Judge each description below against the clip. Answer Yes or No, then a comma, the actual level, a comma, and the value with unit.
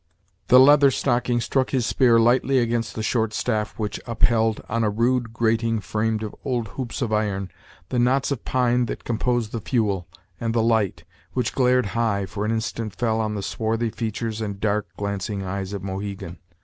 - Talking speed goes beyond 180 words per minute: Yes, average, 190 wpm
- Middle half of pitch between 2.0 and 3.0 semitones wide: Yes, narrow, 2.4 semitones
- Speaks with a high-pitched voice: No, low, 115 Hz